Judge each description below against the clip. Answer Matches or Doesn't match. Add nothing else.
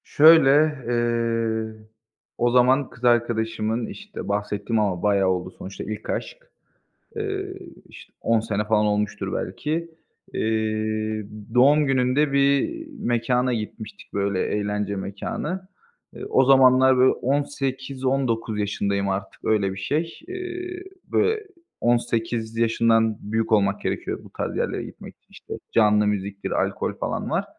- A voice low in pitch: Matches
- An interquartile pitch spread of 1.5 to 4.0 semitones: Doesn't match